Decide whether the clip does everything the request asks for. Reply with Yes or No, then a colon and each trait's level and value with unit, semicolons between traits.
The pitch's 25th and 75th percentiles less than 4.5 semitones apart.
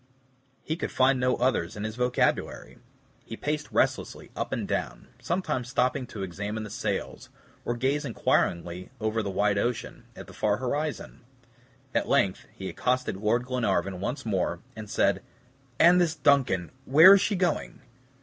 No: average, 5.3 semitones